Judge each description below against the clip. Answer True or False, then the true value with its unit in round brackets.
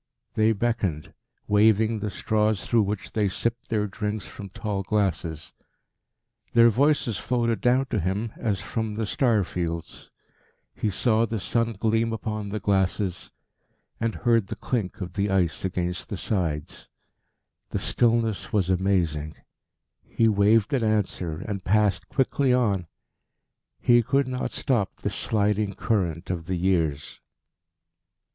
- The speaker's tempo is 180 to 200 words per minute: False (140 wpm)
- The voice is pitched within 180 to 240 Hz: False (105 Hz)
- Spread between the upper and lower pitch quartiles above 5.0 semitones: False (3.3 semitones)